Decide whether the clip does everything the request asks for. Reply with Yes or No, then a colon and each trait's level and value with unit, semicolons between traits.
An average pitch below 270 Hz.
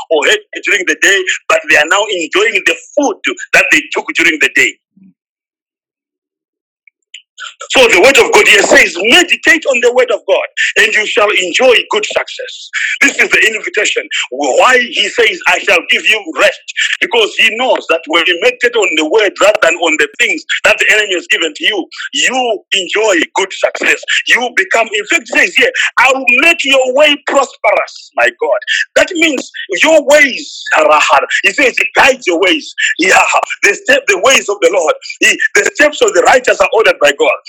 No: very high, 340 Hz